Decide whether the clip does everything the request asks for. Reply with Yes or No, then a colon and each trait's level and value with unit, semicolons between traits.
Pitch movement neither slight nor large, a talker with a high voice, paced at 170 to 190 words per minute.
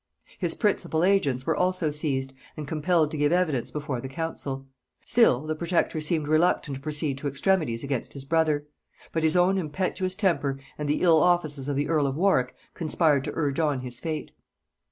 No: average, 3.6 semitones; medium, 155 Hz; average, 185 wpm